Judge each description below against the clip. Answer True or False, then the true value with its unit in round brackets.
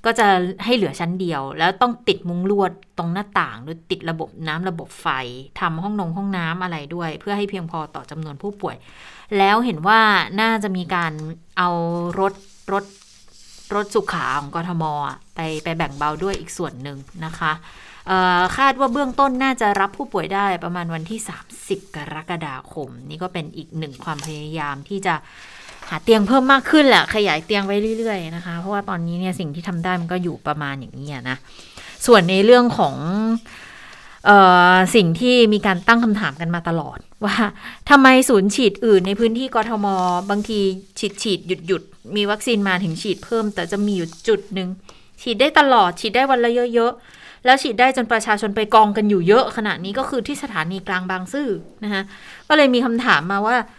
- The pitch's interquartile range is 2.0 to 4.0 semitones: False (4.4 semitones)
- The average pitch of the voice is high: True (195 Hz)